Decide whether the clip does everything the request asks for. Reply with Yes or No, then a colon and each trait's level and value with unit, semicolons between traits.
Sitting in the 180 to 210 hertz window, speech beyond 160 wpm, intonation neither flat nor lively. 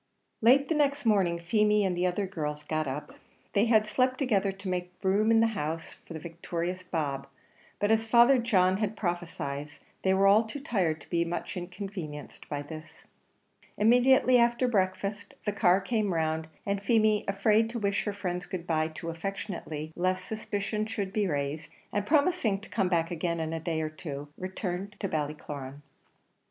Yes: high, 190 Hz; average, 180 wpm; average, 4.6 semitones